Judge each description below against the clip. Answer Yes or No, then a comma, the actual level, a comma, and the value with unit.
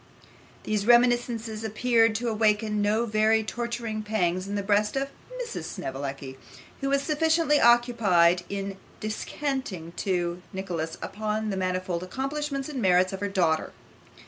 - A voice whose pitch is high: Yes, high, 215 Hz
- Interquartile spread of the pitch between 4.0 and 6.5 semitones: Yes, average, 4.5 semitones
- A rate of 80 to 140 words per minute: Yes, slow, 135 wpm